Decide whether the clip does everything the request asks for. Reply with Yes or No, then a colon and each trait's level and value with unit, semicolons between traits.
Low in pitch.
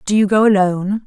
No: high, 200 Hz